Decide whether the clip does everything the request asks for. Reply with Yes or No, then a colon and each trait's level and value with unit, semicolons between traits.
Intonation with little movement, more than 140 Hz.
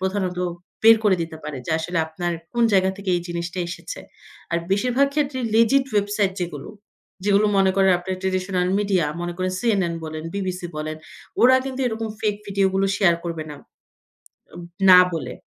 No: average, 3.3 semitones; high, 190 Hz